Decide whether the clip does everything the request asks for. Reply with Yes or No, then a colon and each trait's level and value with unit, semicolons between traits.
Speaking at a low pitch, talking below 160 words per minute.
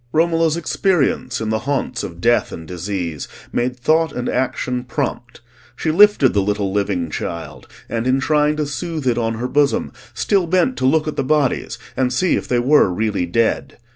No: low, 125 Hz; average, 185 wpm